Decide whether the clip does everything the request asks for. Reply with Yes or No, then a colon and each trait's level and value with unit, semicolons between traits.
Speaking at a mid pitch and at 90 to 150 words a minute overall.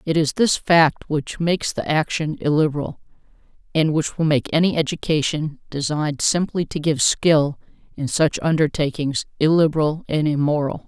Yes: medium, 155 Hz; average, 145 wpm